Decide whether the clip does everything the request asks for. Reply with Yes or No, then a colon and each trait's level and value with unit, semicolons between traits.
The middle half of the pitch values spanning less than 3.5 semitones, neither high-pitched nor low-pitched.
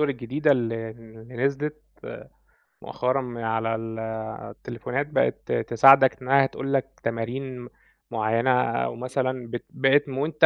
No: average, 3.0 semitones; low, 125 Hz